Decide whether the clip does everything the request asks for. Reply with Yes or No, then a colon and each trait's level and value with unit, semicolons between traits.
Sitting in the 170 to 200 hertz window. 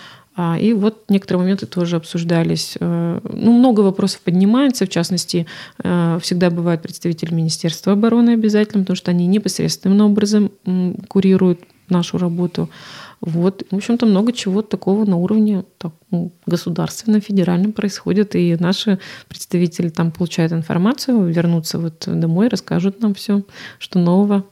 Yes: medium, 185 Hz